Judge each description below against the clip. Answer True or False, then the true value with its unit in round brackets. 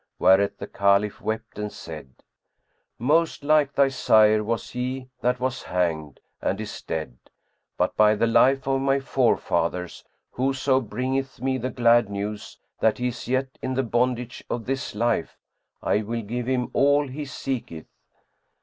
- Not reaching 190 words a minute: True (155 wpm)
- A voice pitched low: True (120 Hz)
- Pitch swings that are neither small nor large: True (3.9 semitones)